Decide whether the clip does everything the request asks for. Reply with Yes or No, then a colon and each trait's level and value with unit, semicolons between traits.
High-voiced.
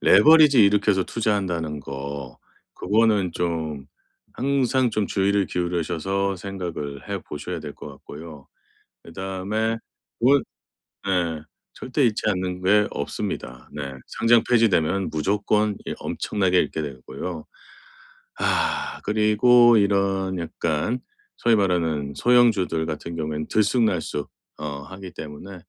No: very low, 95 Hz